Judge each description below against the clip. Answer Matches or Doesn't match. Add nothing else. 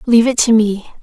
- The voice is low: Doesn't match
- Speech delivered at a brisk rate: Matches